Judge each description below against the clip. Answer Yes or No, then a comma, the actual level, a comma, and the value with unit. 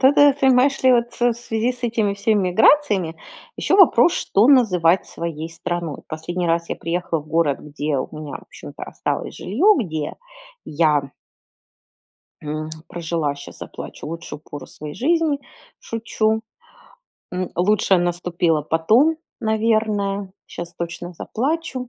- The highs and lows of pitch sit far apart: Yes, wide, 6.6 semitones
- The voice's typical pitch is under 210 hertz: Yes, medium, 185 Hz